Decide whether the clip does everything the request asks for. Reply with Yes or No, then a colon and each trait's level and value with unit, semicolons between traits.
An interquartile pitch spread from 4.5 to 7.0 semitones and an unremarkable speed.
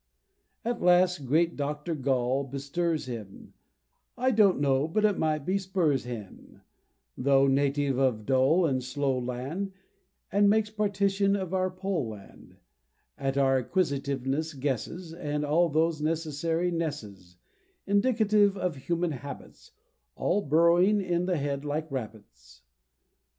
No: average, 5.2 semitones; slow, 130 wpm